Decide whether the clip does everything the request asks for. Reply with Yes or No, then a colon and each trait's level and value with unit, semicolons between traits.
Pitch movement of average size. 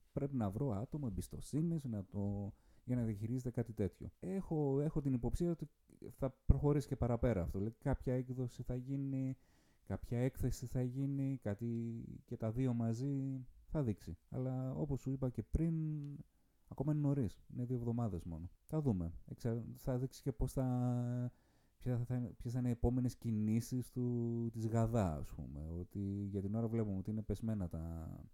Yes: average, 3.8 semitones